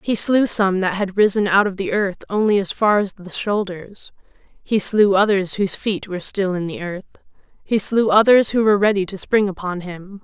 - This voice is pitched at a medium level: No, high, 200 Hz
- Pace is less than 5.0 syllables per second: No, 5.1 syllables/s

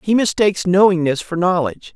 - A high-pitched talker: No, medium, 180 Hz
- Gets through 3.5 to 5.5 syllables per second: No, 6.0 syllables/s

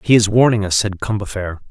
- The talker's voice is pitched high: No, low, 105 Hz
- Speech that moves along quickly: Yes, fast, 210 wpm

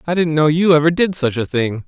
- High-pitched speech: No, medium, 155 Hz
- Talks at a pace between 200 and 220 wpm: No, fast, 290 wpm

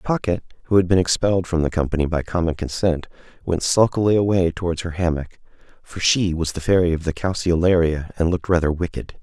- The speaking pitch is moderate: No, very low, 85 Hz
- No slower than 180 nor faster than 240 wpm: Yes, average, 190 wpm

